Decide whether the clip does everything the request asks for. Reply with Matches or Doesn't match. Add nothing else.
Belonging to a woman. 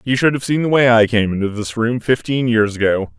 Doesn't match